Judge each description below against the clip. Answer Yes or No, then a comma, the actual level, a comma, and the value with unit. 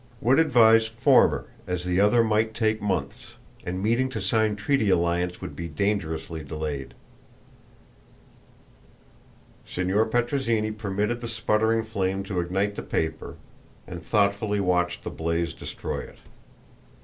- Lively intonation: No, average, 4.0 semitones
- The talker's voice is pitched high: No, low, 105 Hz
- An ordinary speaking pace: No, slow, 125 wpm